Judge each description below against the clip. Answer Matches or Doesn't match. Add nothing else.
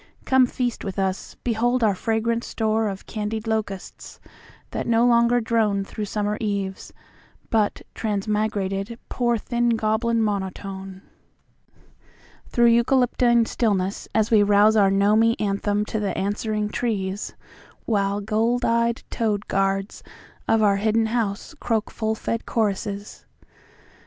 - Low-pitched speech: Doesn't match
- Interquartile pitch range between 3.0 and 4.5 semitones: Doesn't match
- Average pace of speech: Doesn't match